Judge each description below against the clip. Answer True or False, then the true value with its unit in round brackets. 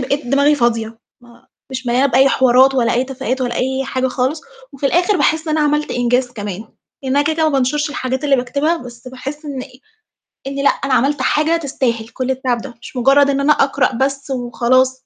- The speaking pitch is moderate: False (265 Hz)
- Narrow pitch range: True (2.3 semitones)